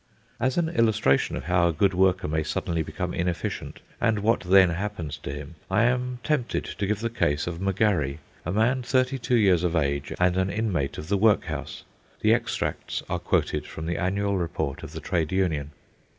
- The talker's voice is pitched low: Yes, very low, 95 Hz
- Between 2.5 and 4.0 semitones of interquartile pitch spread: No, average, 5.0 semitones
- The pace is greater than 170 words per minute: Yes, average, 195 wpm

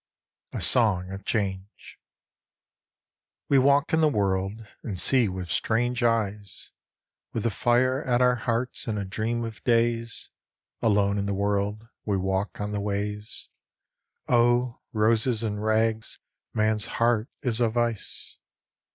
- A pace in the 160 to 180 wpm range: No, average, 140 wpm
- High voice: No, low, 110 Hz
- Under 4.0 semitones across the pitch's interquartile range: Yes, average, 2.8 semitones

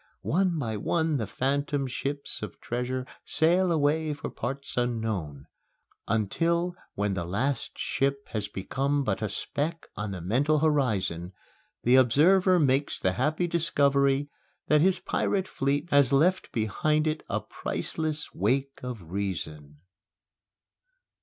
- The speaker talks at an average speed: No, slow, 130 wpm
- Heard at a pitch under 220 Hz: Yes, medium, 140 Hz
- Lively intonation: Yes, wide, 5.9 semitones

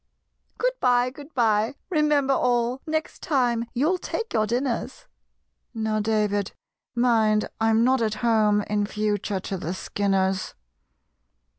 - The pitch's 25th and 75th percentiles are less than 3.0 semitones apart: No, average, 3.7 semitones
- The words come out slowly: Yes, slow, 125 wpm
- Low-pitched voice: No, high, 230 Hz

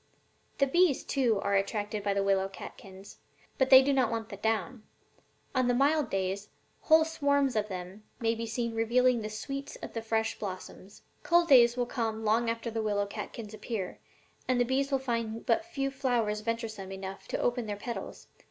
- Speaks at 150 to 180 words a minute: No, average, 190 wpm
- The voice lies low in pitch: No, high, 230 Hz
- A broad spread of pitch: No, average, 3.9 semitones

